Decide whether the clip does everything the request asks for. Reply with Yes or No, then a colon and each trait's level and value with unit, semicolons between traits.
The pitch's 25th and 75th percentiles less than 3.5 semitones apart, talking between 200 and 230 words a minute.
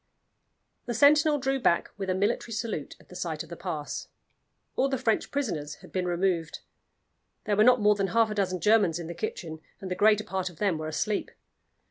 No: average, 4.2 semitones; fast, 205 wpm